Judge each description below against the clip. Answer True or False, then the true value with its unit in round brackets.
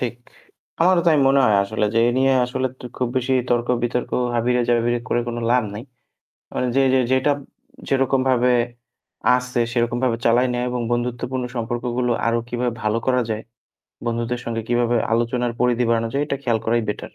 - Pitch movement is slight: True (1.3 semitones)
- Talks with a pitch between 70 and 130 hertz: True (120 Hz)